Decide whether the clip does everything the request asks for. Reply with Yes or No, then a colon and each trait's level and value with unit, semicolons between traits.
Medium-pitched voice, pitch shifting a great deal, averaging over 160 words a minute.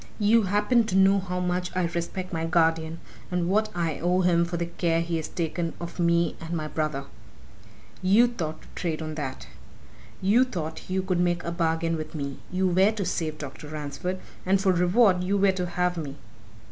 No: medium, 175 Hz; narrow, 2.4 semitones; average, 195 wpm